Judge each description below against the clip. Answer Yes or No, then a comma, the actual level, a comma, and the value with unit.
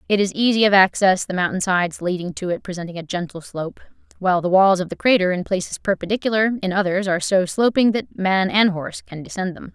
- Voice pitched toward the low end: No, high, 190 Hz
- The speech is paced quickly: Yes, fast, 220 wpm